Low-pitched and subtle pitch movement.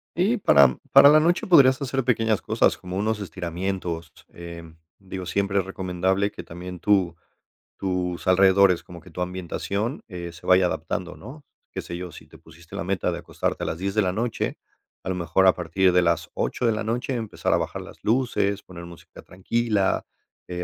No: very low, 95 Hz; average, 3.7 semitones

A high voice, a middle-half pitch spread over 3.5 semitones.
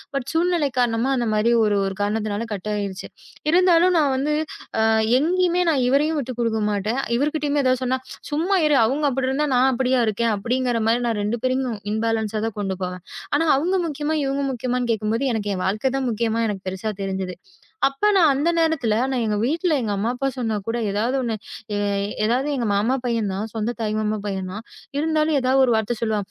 Yes: high, 240 Hz; average, 4.5 semitones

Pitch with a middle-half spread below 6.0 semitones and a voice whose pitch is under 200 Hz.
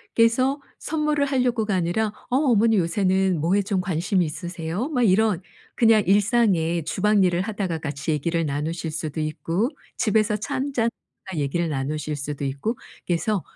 Yes: wide, 5.5 semitones; high, 190 Hz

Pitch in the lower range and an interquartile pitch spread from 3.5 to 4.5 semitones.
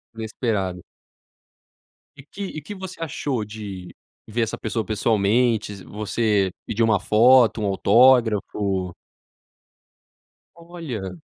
Yes: low, 110 Hz; average, 3.9 semitones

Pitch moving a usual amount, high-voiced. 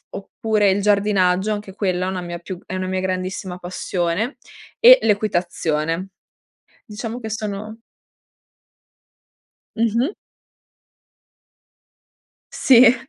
Yes: average, 3.0 semitones; high, 200 Hz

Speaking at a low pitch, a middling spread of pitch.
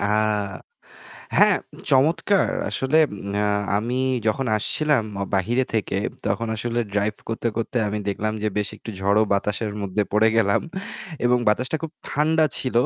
Yes: low, 115 Hz; average, 4.0 semitones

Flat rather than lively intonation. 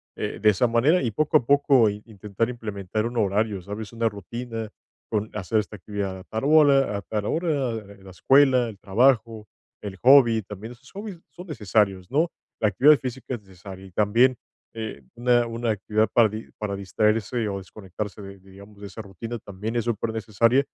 No: average, 3.2 semitones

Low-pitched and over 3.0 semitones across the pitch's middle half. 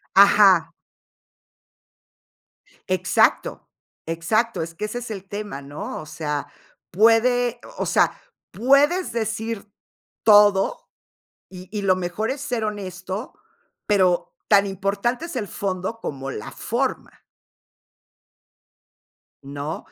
No: high, 200 Hz; average, 3.9 semitones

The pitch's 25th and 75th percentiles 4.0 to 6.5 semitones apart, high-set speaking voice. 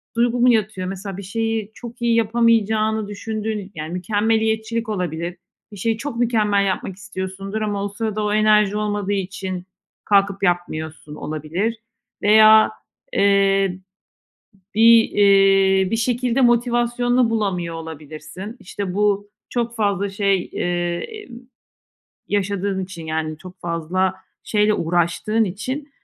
No: average, 3.0 semitones; high, 205 Hz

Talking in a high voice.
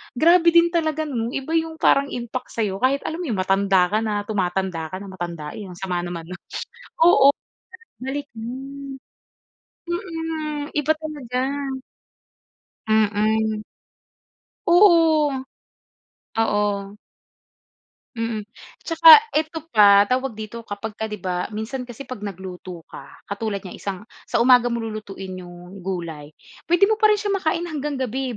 Yes: high, 230 Hz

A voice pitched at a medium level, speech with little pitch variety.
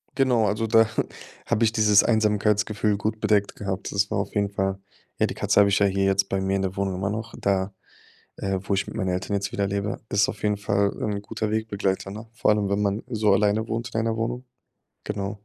No: low, 100 Hz; narrow, 1.7 semitones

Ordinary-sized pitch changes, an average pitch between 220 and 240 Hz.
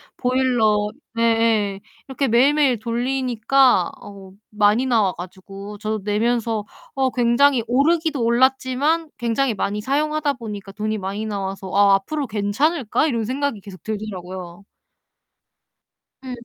Yes: average, 4.4 semitones; high, 230 Hz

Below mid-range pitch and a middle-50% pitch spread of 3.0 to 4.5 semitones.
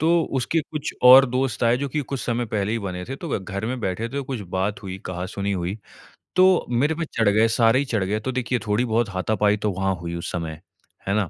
No: low, 110 Hz; average, 4.9 semitones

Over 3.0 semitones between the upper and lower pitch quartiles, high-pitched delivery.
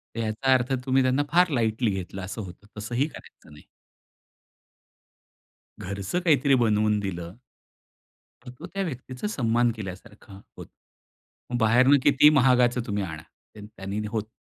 No: average, 4.5 semitones; low, 115 Hz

